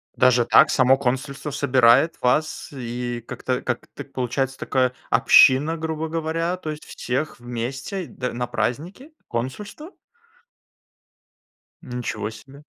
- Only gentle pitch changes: No, average, 4.2 semitones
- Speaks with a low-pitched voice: Yes, low, 130 Hz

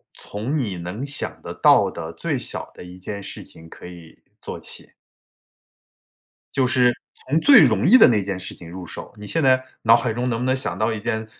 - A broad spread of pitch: Yes, wide, 5.9 semitones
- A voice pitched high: No, low, 110 Hz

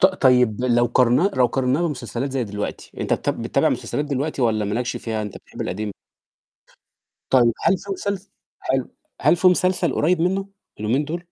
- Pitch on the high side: No, low, 130 Hz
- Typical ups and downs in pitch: No, wide, 6.6 semitones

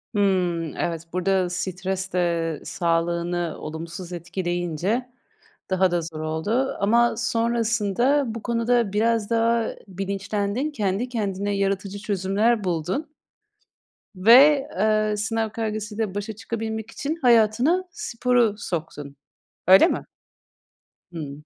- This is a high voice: Yes, high, 205 Hz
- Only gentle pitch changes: No, average, 4.5 semitones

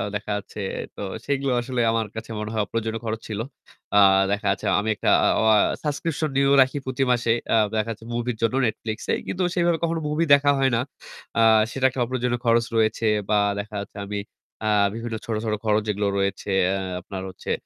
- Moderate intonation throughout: Yes, average, 3.6 semitones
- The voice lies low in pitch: Yes, low, 115 Hz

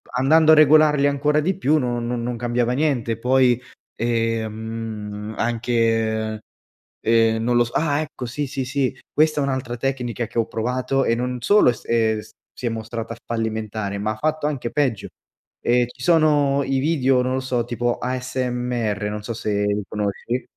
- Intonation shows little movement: No, average, 3.1 semitones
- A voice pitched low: Yes, low, 120 Hz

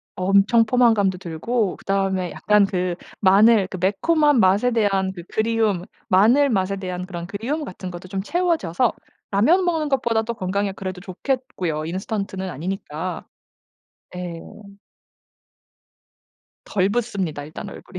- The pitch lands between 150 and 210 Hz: Yes, high, 195 Hz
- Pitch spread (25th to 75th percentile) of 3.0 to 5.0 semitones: Yes, average, 3.7 semitones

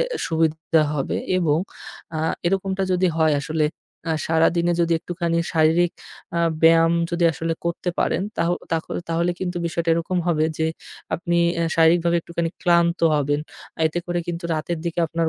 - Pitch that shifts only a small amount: Yes, narrow, 1.2 semitones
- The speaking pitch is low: No, medium, 170 Hz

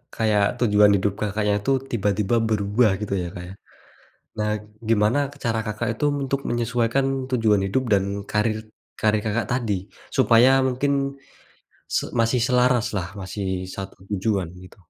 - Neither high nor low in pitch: No, low, 110 Hz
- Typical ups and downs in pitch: Yes, average, 3.4 semitones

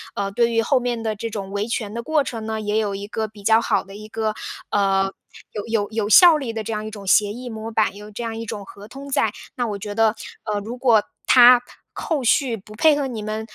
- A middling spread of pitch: No, narrow, 2.3 semitones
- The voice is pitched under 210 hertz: No, high, 220 Hz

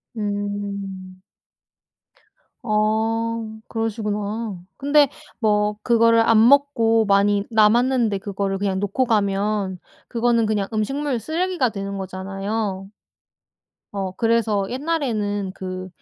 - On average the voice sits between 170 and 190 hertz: No, high, 215 Hz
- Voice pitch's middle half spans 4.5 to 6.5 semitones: No, narrow, 2.5 semitones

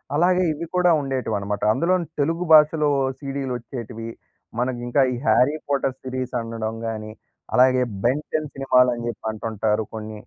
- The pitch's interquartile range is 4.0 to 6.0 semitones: Yes, average, 4.4 semitones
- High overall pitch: No, low, 130 Hz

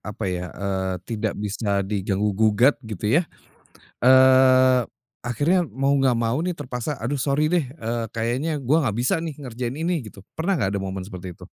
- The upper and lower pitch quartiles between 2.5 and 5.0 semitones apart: No, wide, 5.6 semitones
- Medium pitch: No, low, 125 Hz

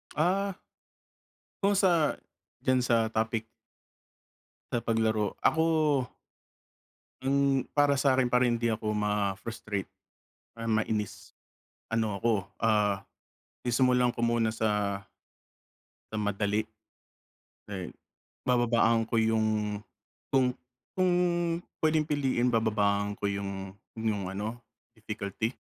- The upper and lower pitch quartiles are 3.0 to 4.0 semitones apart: Yes, average, 3.4 semitones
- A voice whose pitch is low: Yes, low, 115 Hz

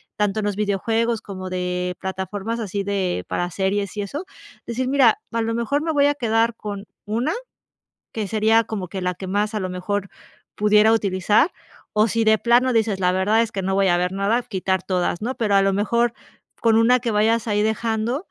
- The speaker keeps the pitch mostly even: No, average, 3.1 semitones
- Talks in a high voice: Yes, high, 210 Hz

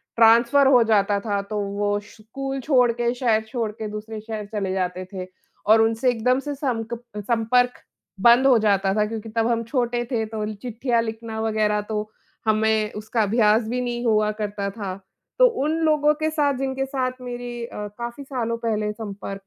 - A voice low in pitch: No, high, 225 Hz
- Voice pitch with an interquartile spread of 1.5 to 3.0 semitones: Yes, average, 2.7 semitones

